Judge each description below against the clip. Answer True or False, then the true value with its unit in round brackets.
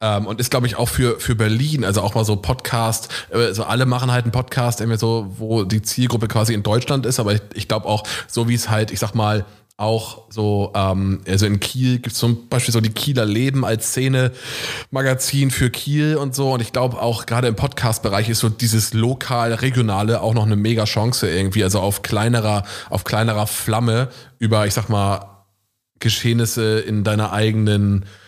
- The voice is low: True (115 Hz)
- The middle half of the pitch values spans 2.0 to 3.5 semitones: True (2.5 semitones)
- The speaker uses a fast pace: True (200 wpm)